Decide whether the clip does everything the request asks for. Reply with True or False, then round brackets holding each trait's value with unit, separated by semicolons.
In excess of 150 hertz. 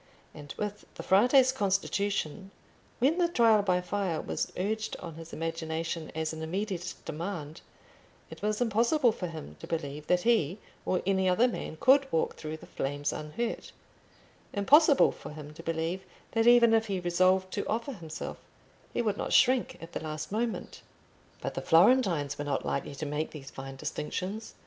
True (185 Hz)